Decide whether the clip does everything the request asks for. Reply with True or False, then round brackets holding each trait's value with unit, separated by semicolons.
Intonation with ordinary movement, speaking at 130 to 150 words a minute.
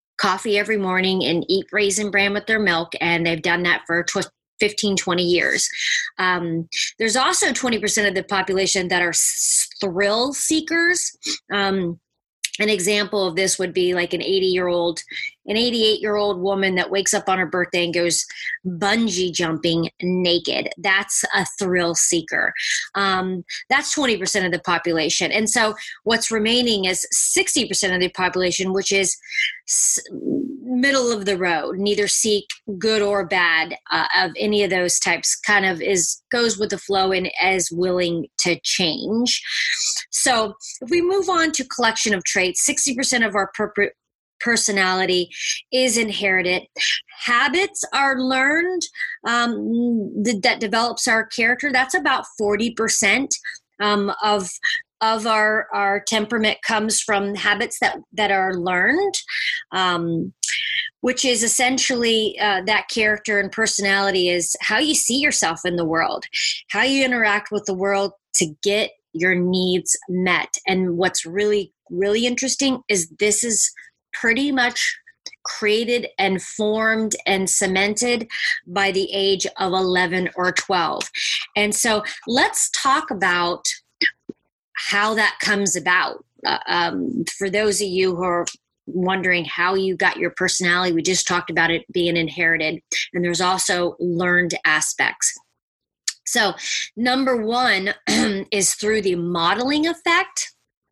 True (4.3 semitones; 145 wpm)